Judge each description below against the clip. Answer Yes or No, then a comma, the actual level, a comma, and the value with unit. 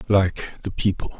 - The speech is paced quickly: No, average, 150 wpm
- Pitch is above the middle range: No, very low, 95 Hz